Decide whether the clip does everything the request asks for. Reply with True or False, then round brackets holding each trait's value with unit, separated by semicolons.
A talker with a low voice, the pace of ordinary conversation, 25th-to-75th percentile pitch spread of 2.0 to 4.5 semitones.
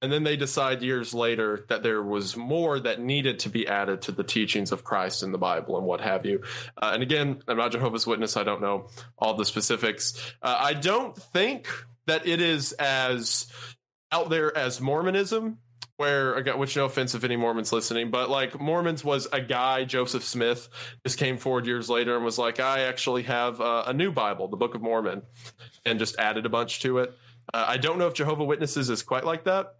False (125 Hz; 215 wpm; 3.0 semitones)